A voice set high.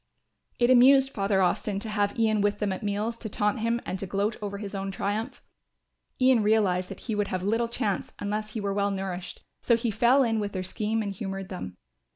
Yes: high, 205 Hz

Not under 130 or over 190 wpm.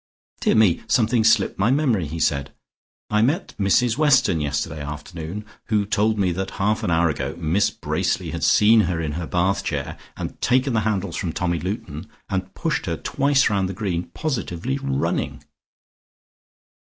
Yes: average, 170 wpm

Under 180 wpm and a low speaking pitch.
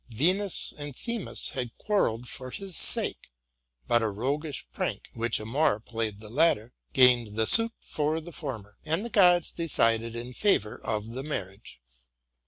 Yes: average, 155 wpm; low, 125 Hz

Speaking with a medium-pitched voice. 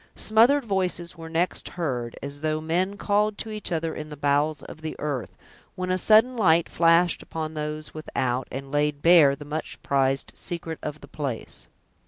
Yes: medium, 160 Hz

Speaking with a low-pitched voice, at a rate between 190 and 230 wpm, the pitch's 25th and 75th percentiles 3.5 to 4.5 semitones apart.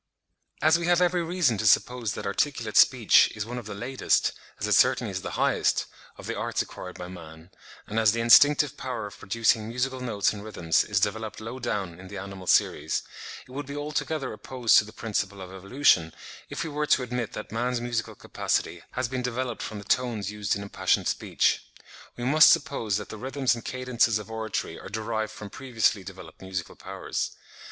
Yes: low, 115 Hz; average, 200 wpm; average, 3.9 semitones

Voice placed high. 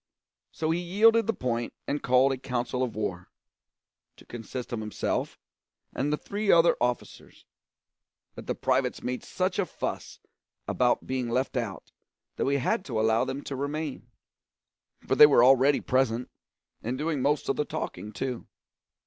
No: low, 130 Hz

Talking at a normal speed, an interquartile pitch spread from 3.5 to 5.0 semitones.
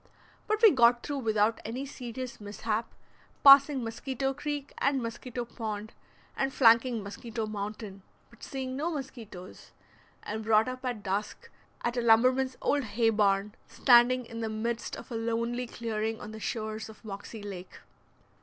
No: average, 155 wpm; average, 2.9 semitones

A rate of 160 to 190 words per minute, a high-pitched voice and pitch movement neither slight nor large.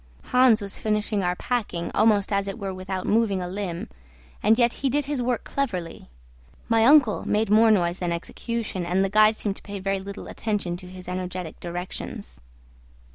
Yes: average, 185 wpm; high, 200 Hz; average, 3.5 semitones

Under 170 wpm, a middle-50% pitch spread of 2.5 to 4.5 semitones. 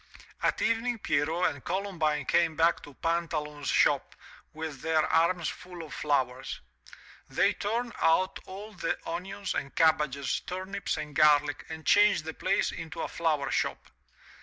Yes: average, 145 wpm; average, 3.8 semitones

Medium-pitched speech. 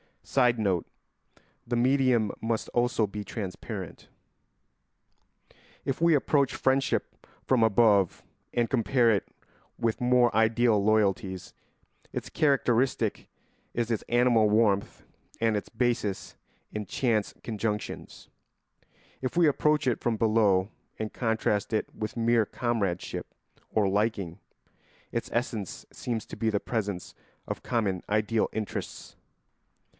No: low, 115 Hz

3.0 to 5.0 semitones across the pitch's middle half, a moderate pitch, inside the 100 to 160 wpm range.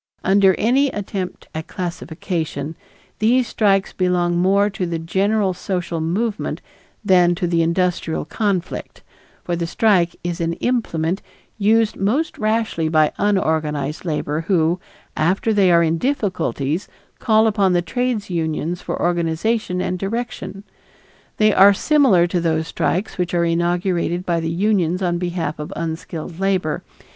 Yes: average, 3.4 semitones; medium, 180 Hz; average, 140 wpm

